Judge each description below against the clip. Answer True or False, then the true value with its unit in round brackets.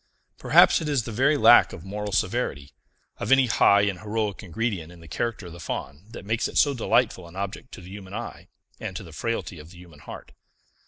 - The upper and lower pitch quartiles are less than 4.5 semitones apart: False (5.0 semitones)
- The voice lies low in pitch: True (100 Hz)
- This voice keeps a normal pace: False (220 wpm)